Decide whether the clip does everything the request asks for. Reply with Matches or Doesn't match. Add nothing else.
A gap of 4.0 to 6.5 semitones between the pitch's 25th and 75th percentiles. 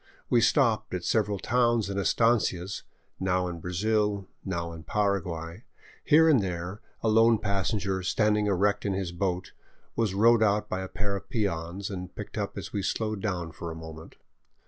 Doesn't match